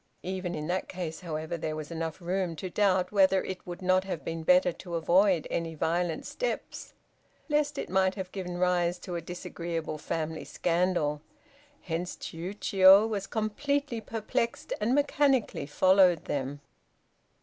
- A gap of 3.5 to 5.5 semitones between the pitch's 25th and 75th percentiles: No, average, 2.7 semitones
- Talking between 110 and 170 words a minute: Yes, average, 150 wpm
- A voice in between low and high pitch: Yes, medium, 180 Hz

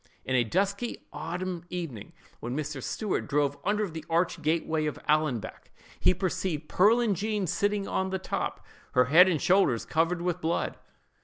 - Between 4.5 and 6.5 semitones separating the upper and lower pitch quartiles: No, average, 4.0 semitones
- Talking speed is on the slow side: No, average, 160 wpm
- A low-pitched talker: No, medium, 170 Hz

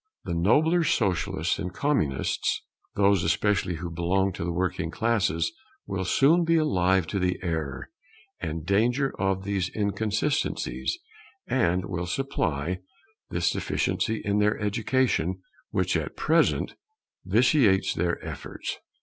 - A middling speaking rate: No, slow, 125 wpm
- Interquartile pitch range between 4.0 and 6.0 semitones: Yes, average, 4.7 semitones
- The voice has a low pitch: Yes, very low, 95 Hz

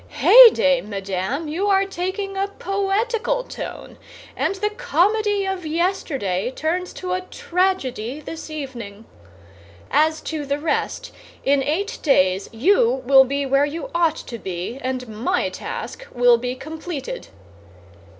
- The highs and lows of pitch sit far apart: Yes, wide, 7.2 semitones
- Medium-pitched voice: No, very high, 310 Hz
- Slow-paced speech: Yes, slow, 130 wpm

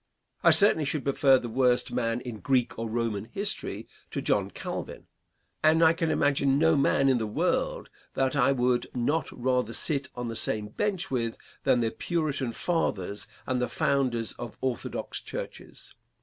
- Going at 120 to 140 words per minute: No, average, 165 wpm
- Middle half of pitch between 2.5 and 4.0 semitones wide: Yes, average, 3.5 semitones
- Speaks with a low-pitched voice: Yes, low, 130 Hz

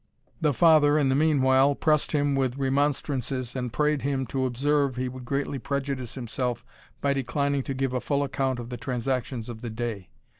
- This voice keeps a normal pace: Yes, average, 185 wpm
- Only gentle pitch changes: Yes, narrow, 2.1 semitones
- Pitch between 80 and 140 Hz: Yes, low, 135 Hz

